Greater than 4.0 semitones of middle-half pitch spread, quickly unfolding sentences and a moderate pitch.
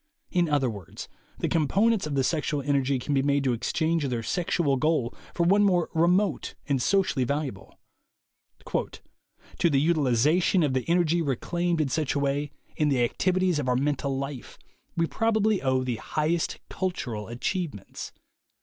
No: average, 4.5 semitones; average, 160 wpm; medium, 150 Hz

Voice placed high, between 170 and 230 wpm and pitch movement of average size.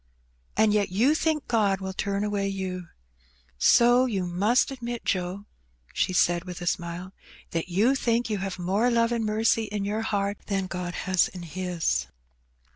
Yes: high, 200 Hz; average, 175 wpm; average, 3.7 semitones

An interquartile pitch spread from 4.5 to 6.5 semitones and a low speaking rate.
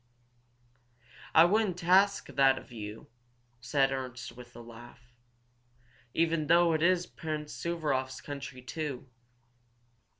Yes: average, 4.9 semitones; slow, 110 wpm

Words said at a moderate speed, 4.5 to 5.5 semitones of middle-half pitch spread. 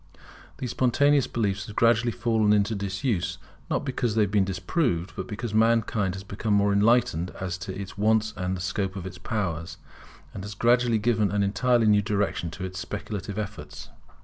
No: average, 180 wpm; average, 3.1 semitones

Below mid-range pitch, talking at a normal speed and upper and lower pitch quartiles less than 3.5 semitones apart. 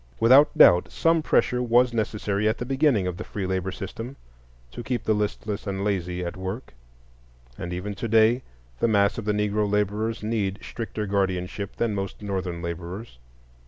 Yes: low, 105 Hz; average, 170 wpm; average, 3.1 semitones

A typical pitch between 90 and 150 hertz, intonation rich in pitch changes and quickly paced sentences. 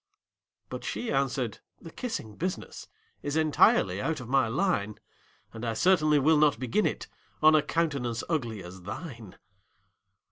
No: low, 135 Hz; wide, 5.9 semitones; average, 145 wpm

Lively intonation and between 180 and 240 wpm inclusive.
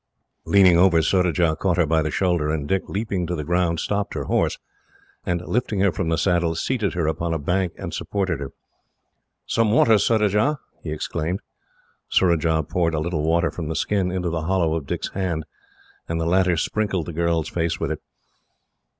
No: average, 2.8 semitones; average, 185 wpm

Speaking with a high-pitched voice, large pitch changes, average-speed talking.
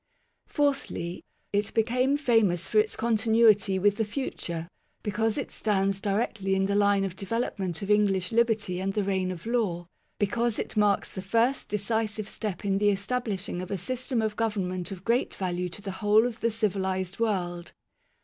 No: high, 205 Hz; average, 2.9 semitones; average, 180 wpm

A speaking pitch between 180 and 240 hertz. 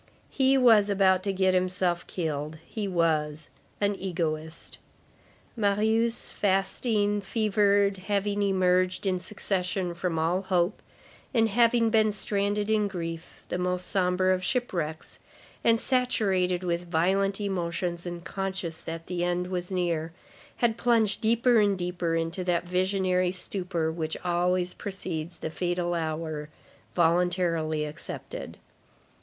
Yes: medium, 185 Hz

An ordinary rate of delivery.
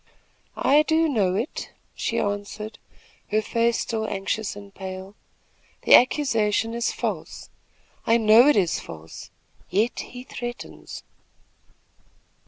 No: slow, 115 wpm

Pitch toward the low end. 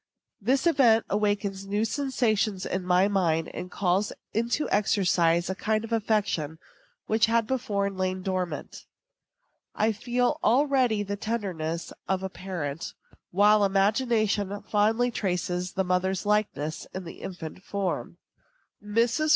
No: high, 205 Hz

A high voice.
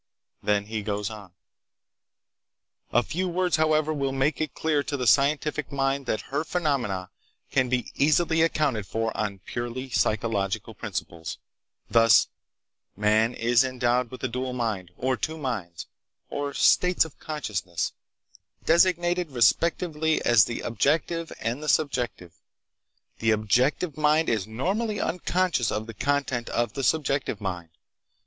No: low, 130 Hz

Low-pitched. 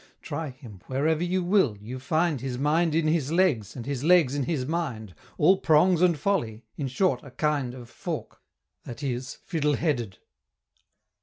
No: medium, 145 Hz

